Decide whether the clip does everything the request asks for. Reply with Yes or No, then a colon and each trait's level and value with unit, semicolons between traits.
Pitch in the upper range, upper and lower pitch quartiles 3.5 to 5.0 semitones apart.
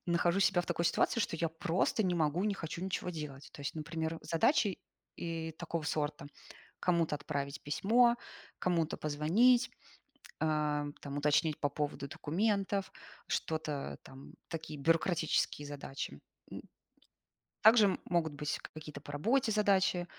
No: medium, 165 Hz; average, 3.9 semitones